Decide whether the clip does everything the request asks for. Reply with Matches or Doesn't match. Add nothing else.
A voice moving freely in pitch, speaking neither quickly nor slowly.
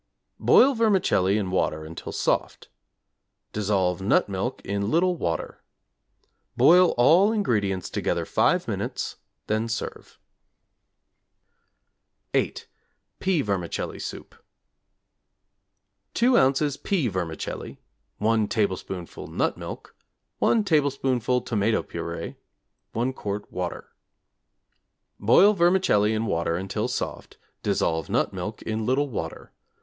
Doesn't match